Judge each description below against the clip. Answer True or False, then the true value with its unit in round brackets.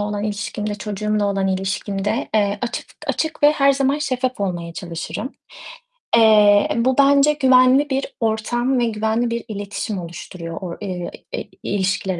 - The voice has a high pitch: True (215 Hz)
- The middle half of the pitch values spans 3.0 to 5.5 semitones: True (4.5 semitones)